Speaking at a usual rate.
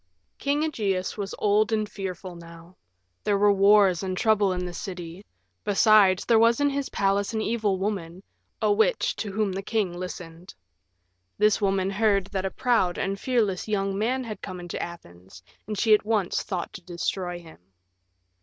Yes: average, 175 wpm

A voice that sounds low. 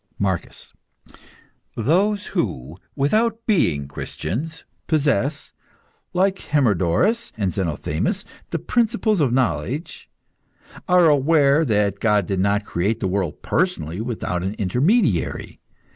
Yes: low, 125 Hz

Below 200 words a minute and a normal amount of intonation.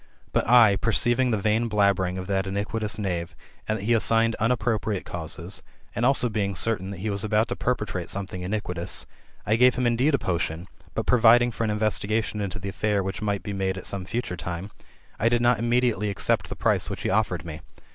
No: fast, 205 wpm; average, 3.1 semitones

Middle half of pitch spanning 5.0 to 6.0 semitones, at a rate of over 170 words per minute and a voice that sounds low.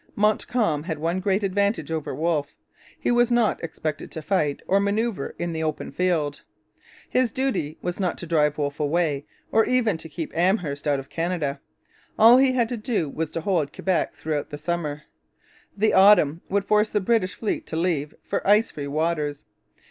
No: wide, 5.4 semitones; average, 180 wpm; medium, 170 Hz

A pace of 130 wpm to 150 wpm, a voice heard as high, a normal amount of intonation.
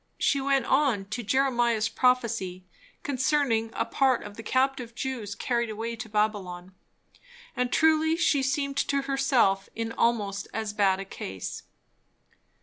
Yes: average, 140 wpm; high, 235 Hz; average, 4.4 semitones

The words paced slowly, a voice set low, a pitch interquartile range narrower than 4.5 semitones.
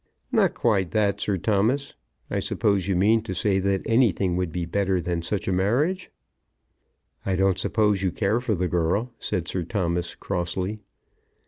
No: average, 165 wpm; very low, 95 Hz; average, 3.0 semitones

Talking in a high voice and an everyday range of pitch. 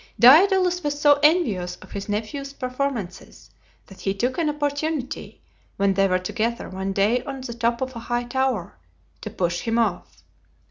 No: high, 240 Hz; wide, 6.3 semitones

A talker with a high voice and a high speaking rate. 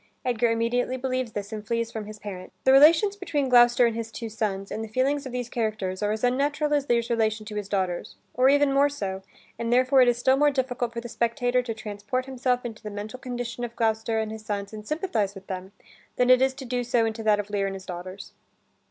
Yes: high, 235 Hz; fast, 240 wpm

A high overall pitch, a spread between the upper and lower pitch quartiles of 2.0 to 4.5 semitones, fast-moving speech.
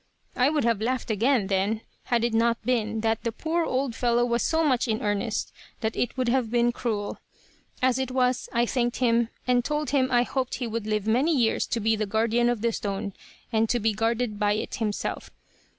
Yes: high, 235 Hz; narrow, 2.4 semitones; fast, 215 wpm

